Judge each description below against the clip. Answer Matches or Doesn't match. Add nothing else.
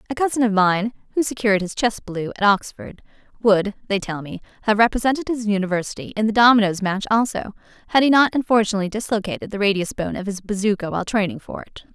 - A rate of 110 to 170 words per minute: Doesn't match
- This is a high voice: Matches